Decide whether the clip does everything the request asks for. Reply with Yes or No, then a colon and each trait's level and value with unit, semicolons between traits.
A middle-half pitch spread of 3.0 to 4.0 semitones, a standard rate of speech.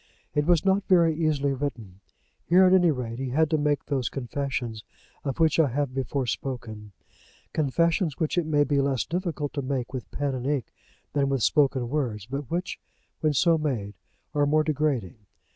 Yes: average, 3.4 semitones; average, 180 wpm